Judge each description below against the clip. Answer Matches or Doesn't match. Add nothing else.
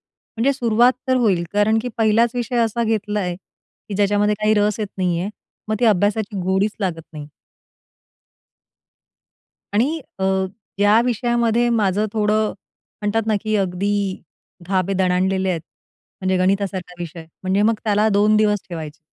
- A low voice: Doesn't match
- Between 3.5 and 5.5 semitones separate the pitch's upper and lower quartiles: Doesn't match